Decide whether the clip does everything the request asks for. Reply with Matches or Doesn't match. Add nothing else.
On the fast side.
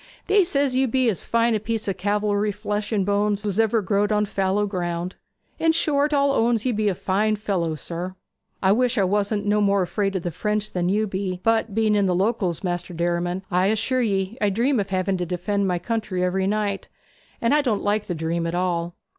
Matches